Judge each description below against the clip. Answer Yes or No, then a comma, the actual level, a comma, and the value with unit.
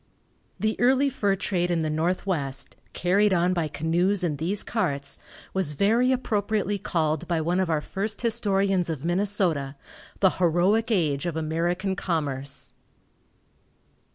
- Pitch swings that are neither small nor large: Yes, average, 4.2 semitones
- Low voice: No, medium, 180 Hz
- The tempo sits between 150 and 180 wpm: No, slow, 135 wpm